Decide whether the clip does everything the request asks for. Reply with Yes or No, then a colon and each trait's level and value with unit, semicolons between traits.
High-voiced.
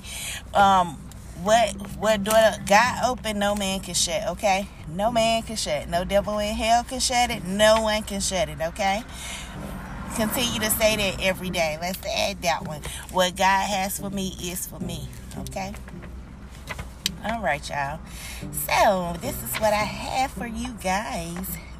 Yes: high, 200 Hz